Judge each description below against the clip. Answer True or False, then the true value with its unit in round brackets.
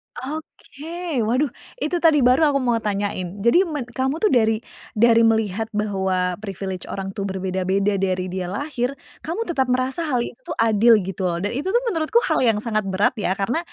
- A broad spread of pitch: True (6.1 semitones)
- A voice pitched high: True (225 Hz)